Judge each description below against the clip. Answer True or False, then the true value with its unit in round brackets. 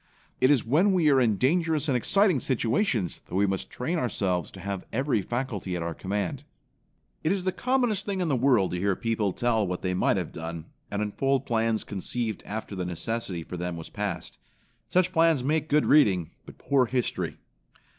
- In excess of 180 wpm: True (195 wpm)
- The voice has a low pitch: True (115 Hz)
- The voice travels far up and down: True (7.6 semitones)